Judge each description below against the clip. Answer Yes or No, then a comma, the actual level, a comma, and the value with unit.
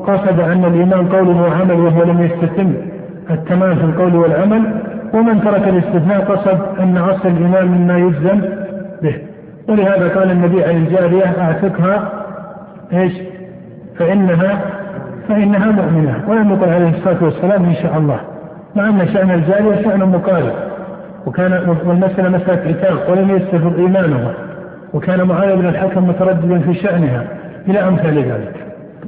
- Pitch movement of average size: No, narrow, 2.0 semitones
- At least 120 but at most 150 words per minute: Yes, average, 130 wpm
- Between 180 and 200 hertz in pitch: Yes, medium, 185 Hz